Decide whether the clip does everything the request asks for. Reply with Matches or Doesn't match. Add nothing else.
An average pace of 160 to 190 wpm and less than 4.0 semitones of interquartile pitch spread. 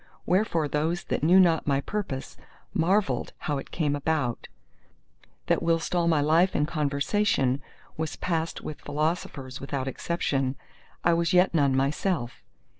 Doesn't match